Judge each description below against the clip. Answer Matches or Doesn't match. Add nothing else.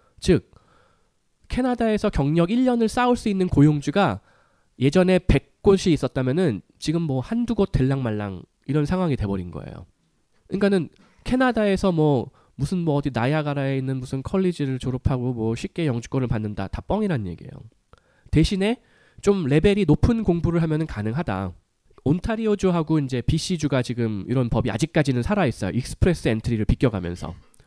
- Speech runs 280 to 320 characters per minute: Doesn't match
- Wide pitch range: Matches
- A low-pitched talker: Doesn't match